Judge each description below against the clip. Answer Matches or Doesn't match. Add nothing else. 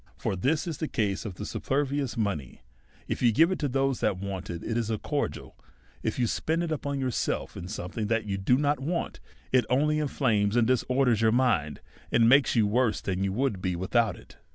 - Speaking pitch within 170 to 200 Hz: Doesn't match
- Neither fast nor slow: Doesn't match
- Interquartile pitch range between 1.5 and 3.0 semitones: Doesn't match